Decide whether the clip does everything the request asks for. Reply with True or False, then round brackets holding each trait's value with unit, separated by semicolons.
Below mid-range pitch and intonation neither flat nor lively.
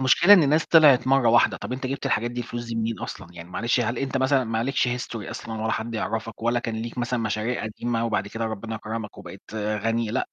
False (115 Hz; 2.1 semitones)